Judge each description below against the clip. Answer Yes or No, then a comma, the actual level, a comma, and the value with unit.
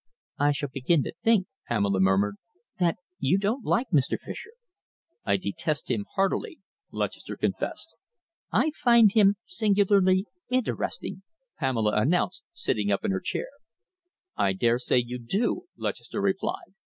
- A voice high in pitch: No, medium, 145 Hz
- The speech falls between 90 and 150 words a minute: Yes, slow, 135 wpm